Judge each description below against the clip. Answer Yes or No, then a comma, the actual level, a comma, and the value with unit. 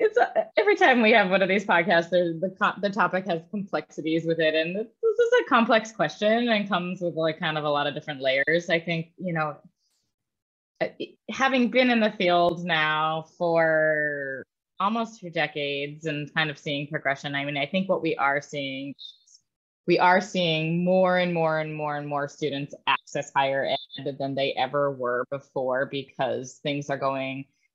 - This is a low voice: No, medium, 160 Hz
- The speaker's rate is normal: Yes, average, 180 wpm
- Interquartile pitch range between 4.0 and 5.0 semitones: Yes, average, 4.3 semitones